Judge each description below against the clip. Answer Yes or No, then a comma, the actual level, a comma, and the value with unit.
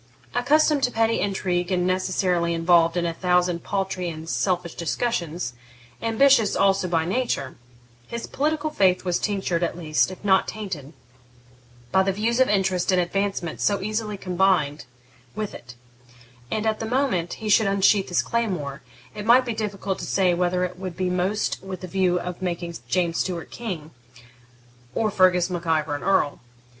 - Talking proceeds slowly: No, average, 170 wpm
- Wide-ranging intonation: No, average, 3.3 semitones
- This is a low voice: No, medium, 185 Hz